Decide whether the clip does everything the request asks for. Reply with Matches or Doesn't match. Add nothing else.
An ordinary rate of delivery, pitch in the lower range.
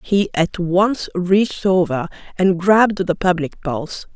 Doesn't match